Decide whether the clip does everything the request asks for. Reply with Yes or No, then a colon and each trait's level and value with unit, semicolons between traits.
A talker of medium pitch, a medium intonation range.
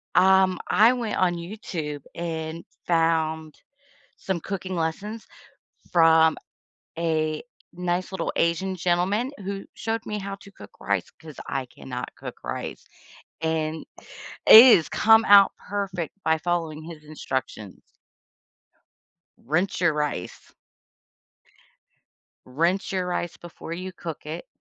Yes: medium, 170 Hz; average, 3.3 semitones